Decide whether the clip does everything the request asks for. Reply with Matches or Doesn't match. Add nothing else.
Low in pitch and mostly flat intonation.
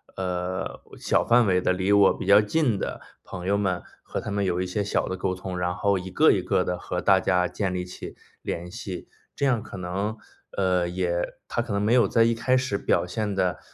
Matches